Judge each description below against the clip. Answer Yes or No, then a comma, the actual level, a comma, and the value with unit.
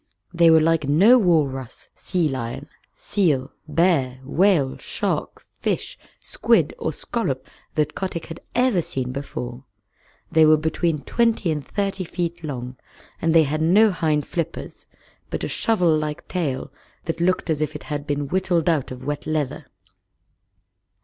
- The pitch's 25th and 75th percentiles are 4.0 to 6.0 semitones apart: No, average, 3.6 semitones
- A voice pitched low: No, medium, 155 Hz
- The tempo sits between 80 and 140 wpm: No, average, 150 wpm